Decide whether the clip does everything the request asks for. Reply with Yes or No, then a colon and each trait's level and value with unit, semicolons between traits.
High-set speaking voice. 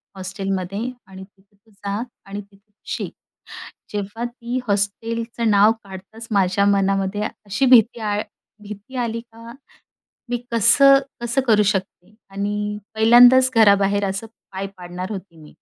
Yes: high, 205 Hz